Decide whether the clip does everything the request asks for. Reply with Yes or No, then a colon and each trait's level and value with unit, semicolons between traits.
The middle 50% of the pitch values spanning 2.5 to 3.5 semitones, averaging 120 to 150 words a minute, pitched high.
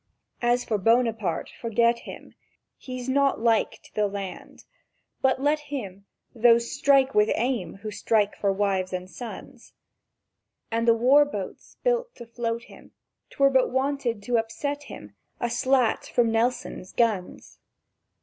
No: average, 3.9 semitones; average, 140 wpm; high, 235 Hz